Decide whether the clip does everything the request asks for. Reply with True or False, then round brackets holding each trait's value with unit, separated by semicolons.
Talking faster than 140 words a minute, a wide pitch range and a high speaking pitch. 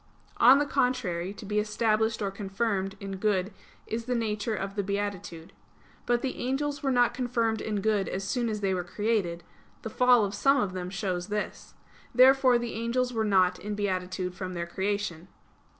False (180 wpm; 3.8 semitones; 210 Hz)